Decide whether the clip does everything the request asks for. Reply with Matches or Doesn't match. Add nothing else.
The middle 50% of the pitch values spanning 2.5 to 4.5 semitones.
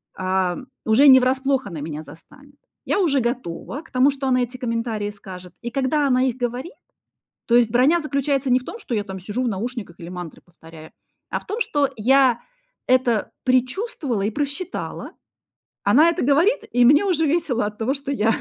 Doesn't match